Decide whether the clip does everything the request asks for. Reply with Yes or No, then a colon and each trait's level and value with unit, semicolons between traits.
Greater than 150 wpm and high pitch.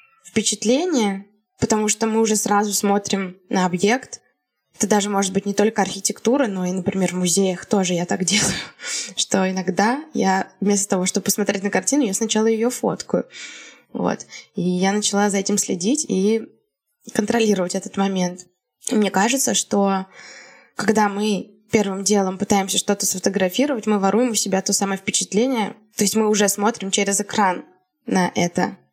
Yes: fast, 160 wpm; high, 205 Hz